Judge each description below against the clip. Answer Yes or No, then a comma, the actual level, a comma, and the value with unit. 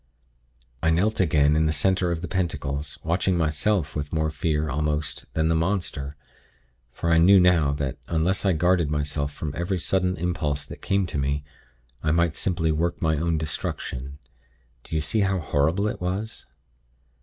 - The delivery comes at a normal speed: Yes, average, 175 wpm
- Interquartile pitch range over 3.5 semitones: No, average, 3.2 semitones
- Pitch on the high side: No, very low, 80 Hz